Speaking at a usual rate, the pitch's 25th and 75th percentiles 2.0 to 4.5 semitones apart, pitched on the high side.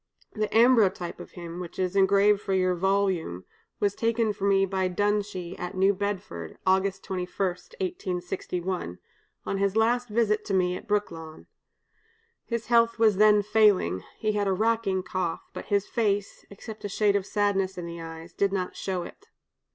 Yes: average, 165 wpm; narrow, 2.4 semitones; high, 195 Hz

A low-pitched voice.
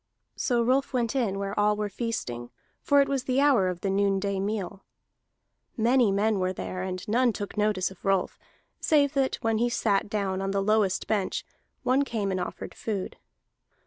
No: high, 210 Hz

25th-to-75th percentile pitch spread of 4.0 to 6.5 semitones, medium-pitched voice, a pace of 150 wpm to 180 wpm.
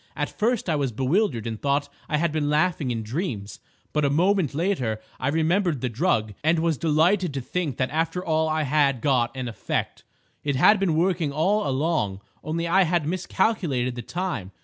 No: average, 5.1 semitones; medium, 155 Hz; average, 190 wpm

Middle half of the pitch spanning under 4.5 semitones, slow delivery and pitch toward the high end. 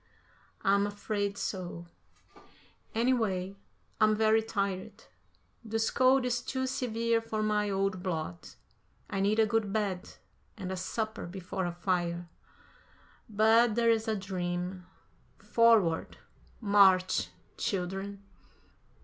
Yes: average, 3.1 semitones; slow, 105 wpm; high, 200 Hz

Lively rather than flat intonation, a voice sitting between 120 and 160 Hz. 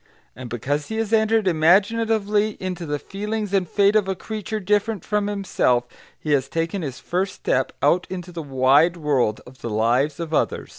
No: wide, 6.2 semitones; medium, 180 Hz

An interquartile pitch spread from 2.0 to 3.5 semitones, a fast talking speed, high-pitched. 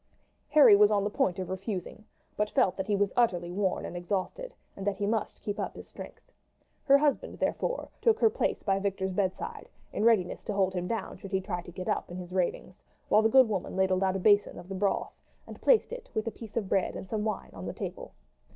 Yes: average, 2.8 semitones; fast, 240 wpm; high, 200 Hz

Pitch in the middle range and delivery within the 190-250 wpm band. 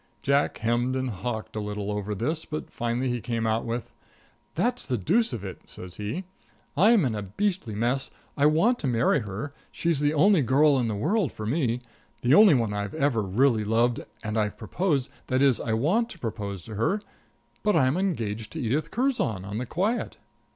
No: low, 125 Hz; average, 200 wpm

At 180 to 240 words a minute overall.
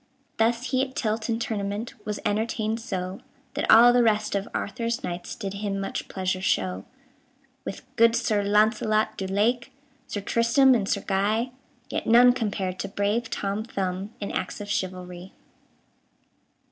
No: average, 155 wpm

